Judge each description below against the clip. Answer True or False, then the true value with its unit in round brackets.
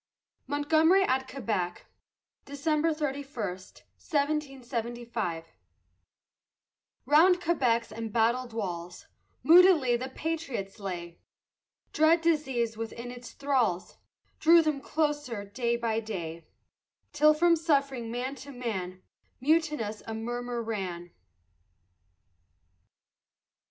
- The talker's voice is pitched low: False (245 Hz)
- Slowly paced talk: True (90 wpm)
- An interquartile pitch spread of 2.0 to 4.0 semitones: False (5.4 semitones)